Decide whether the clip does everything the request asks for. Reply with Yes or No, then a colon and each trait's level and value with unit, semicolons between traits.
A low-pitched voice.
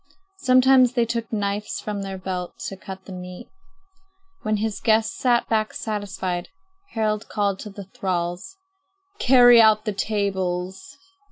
No: high, 210 Hz